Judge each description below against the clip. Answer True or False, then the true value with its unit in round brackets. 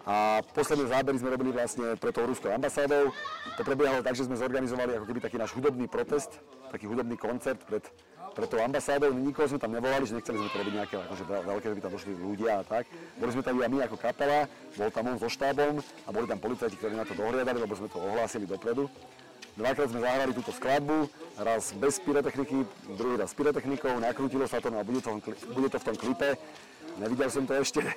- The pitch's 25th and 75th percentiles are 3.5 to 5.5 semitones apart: True (4.0 semitones)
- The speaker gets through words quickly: True (215 wpm)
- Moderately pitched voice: False (125 Hz)